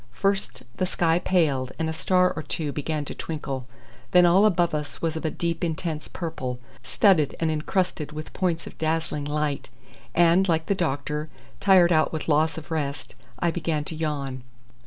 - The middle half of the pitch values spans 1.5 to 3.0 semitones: Yes, narrow, 2.5 semitones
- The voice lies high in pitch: No, medium, 160 Hz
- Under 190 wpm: Yes, average, 180 wpm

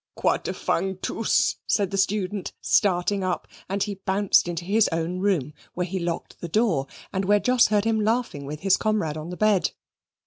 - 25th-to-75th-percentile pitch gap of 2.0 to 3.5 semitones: Yes, average, 3.1 semitones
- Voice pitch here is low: No, high, 190 Hz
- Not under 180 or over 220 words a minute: Yes, average, 185 wpm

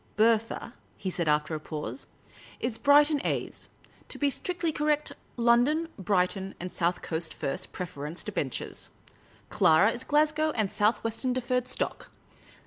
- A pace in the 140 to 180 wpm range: Yes, average, 150 wpm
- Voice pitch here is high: Yes, high, 225 Hz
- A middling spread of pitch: No, wide, 8.3 semitones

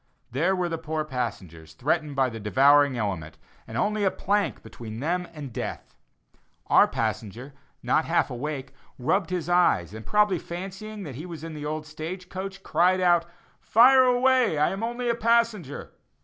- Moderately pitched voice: Yes, medium, 165 Hz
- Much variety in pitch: Yes, wide, 6.5 semitones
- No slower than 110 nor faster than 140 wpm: No, average, 165 wpm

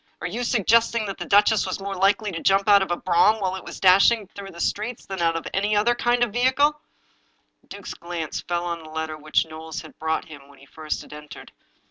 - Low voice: No, high, 190 Hz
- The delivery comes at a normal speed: No, fast, 240 wpm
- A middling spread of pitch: Yes, average, 4.7 semitones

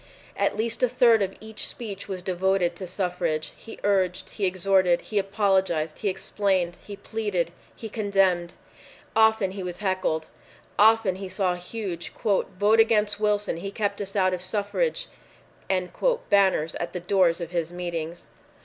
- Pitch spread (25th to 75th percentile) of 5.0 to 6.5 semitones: No, average, 2.8 semitones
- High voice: Yes, high, 195 Hz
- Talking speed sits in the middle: Yes, average, 150 wpm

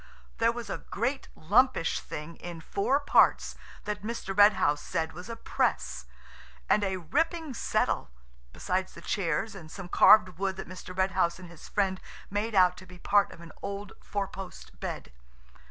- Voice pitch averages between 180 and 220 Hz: Yes, high, 190 Hz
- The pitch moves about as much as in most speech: Yes, average, 3.5 semitones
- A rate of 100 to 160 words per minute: No, average, 170 wpm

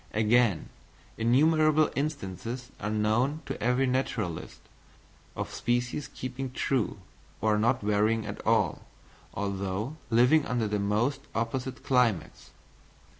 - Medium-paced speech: No, slow, 110 wpm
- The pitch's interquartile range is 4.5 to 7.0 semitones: No, average, 3.8 semitones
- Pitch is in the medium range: No, low, 120 Hz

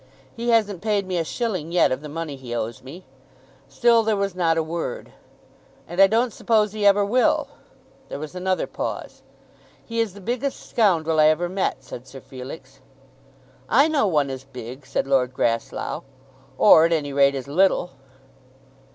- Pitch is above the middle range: No, medium, 170 Hz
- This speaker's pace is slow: No, average, 175 wpm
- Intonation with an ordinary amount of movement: No, wide, 6.8 semitones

